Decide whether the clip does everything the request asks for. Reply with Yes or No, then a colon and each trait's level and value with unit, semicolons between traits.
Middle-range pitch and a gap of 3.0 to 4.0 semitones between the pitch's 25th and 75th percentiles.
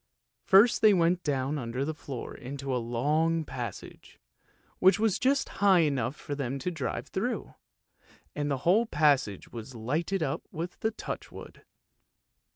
No: medium, 150 Hz; average, 5.2 semitones